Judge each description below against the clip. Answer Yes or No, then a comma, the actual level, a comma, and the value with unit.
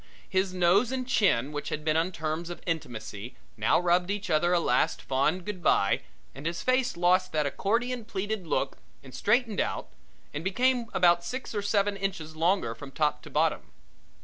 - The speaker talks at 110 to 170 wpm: No, average, 180 wpm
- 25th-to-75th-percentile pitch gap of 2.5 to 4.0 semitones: No, average, 4.8 semitones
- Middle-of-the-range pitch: Yes, medium, 175 Hz